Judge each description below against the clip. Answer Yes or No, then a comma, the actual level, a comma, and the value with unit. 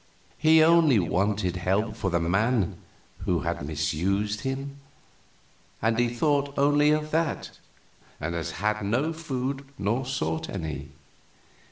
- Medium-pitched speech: No, low, 110 Hz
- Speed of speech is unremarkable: No, slow, 130 wpm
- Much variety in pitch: Yes, wide, 7.5 semitones